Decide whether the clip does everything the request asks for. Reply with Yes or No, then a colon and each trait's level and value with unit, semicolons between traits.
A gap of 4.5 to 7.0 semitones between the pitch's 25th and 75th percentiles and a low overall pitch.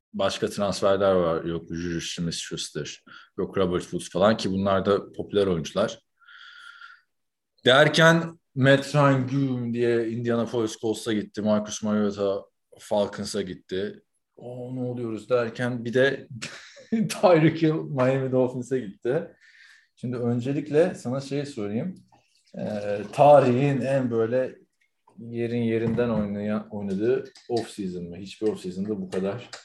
Yes: average, 4.9 semitones; low, 120 Hz